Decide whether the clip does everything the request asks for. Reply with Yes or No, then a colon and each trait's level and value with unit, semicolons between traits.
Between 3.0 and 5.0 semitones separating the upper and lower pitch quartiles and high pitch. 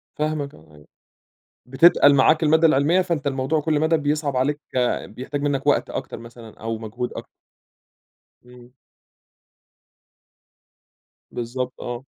No: average, 3.8 semitones; medium, 140 Hz